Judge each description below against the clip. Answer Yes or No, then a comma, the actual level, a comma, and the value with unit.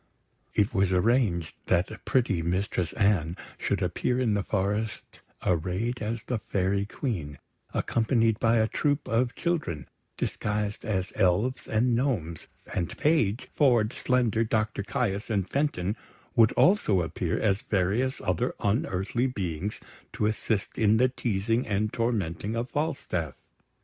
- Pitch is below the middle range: Yes, low, 105 Hz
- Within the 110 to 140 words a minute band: Yes, slow, 135 wpm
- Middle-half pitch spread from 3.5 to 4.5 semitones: Yes, average, 4.1 semitones